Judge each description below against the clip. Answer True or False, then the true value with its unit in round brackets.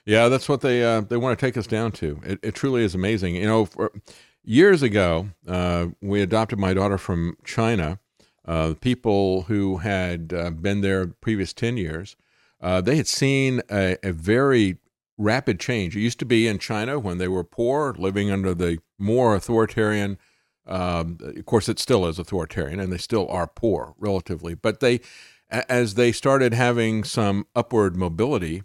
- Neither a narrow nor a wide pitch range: True (4.2 semitones)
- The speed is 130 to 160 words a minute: False (180 wpm)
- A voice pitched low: True (100 Hz)